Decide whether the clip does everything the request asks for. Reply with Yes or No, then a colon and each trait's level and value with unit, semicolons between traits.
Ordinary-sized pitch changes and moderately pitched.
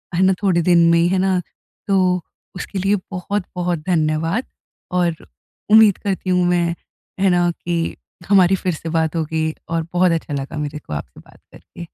No: narrow, 2.2 semitones; medium, 175 Hz